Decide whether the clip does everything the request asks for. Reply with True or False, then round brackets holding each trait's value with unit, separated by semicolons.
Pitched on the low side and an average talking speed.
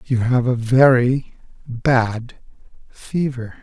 False (125 Hz; 100 wpm)